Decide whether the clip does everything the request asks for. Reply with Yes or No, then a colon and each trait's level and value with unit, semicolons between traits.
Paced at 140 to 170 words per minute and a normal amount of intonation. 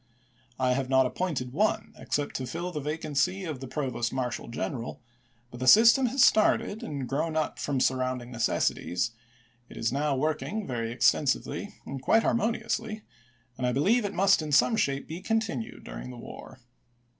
No: average, 165 wpm; wide, 6.9 semitones